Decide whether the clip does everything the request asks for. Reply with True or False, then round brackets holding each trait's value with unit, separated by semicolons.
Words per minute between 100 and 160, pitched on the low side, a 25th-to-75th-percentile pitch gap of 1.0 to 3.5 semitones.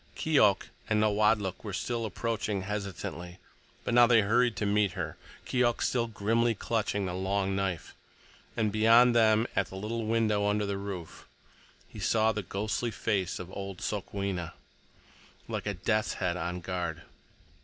True (150 wpm; 105 Hz; 2.8 semitones)